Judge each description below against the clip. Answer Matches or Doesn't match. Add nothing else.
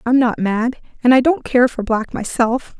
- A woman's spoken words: Matches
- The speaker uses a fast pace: Matches